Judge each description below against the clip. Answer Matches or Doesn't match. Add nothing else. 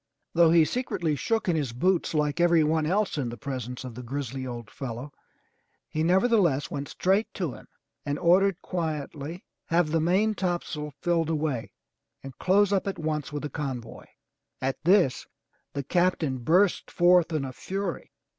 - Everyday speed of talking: Matches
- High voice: Doesn't match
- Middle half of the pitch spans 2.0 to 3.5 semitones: Doesn't match